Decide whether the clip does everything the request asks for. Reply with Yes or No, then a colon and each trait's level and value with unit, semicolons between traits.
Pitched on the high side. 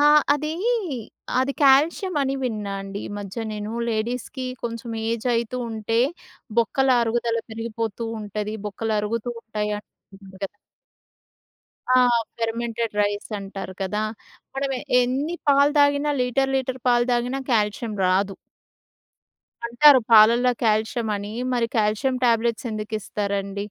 Yes: high, 230 Hz